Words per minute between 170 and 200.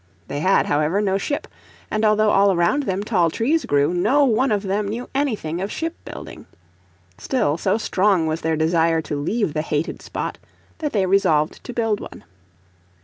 Yes: average, 180 wpm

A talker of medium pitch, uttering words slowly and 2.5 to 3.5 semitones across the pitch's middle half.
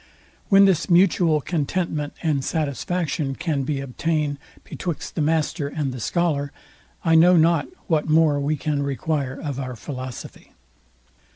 Yes: medium, 150 Hz; slow, 130 wpm; average, 2.8 semitones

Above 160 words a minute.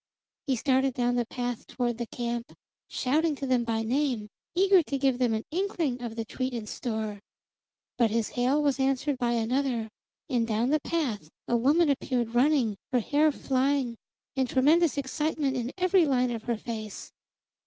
Yes: average, 175 wpm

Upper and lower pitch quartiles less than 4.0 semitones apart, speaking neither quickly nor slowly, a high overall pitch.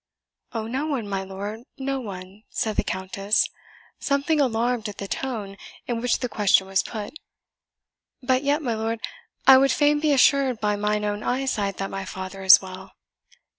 No: average, 5.0 semitones; average, 170 wpm; high, 220 Hz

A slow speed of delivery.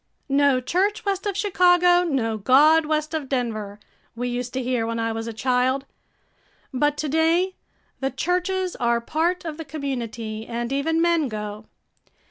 No: average, 160 wpm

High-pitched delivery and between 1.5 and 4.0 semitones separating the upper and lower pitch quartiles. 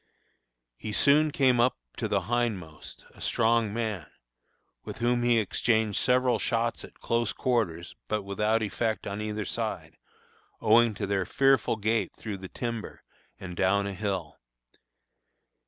No: low, 110 Hz; average, 3.0 semitones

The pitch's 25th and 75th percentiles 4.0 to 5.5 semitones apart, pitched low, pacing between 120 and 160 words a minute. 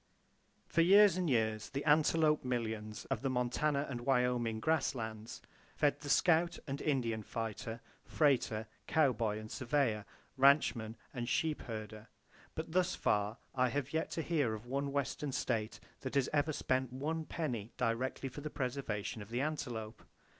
Yes: average, 4.7 semitones; low, 130 Hz; average, 155 wpm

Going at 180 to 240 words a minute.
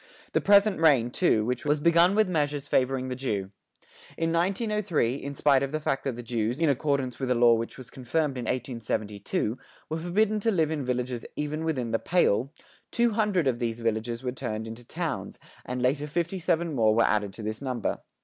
Yes: average, 195 wpm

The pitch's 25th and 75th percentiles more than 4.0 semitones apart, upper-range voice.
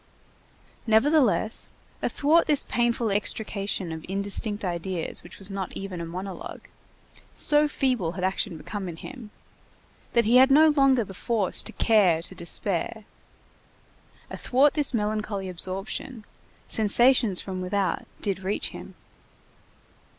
Yes: average, 4.4 semitones; high, 205 Hz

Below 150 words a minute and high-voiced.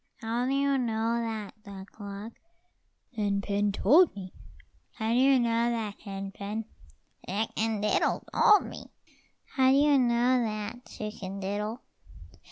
Yes: average, 140 wpm; high, 220 Hz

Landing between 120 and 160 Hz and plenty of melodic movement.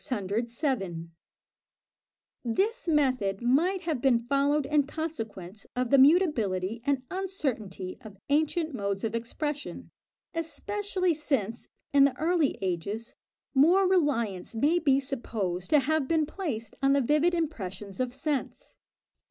No: very high, 275 Hz; wide, 5.8 semitones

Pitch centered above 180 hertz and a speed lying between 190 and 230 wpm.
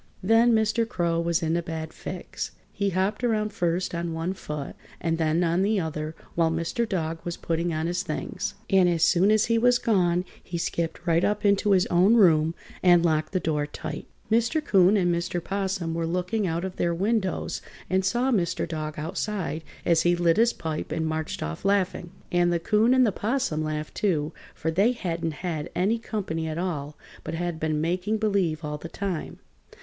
No: medium, 175 Hz; average, 195 wpm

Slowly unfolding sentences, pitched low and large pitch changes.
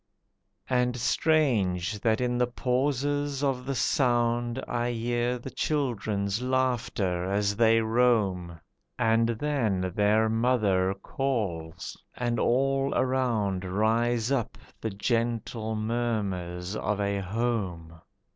No: slow, 110 wpm; low, 115 Hz; average, 3.7 semitones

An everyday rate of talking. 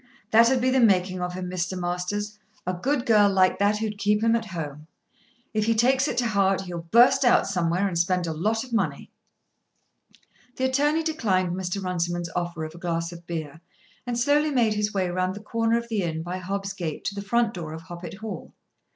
No: fast, 210 wpm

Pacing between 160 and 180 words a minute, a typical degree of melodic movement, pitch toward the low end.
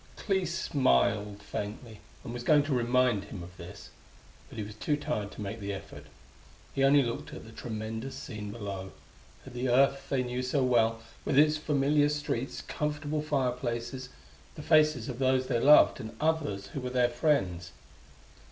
Yes: average, 175 wpm; average, 4.7 semitones; low, 125 Hz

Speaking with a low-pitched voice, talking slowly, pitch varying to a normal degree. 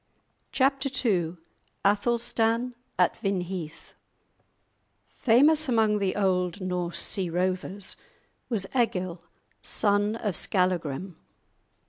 No: high, 195 Hz; slow, 85 wpm; average, 4.0 semitones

